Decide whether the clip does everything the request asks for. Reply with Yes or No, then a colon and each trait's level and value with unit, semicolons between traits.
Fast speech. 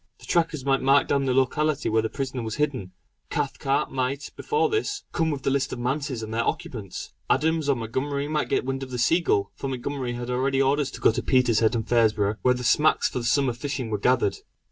Yes: fast, 220 wpm